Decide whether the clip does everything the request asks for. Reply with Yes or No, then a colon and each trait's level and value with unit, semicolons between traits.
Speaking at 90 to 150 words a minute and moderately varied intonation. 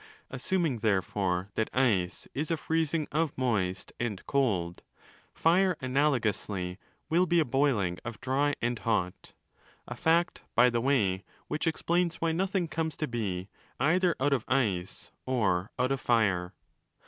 No: average, 145 wpm; wide, 7.9 semitones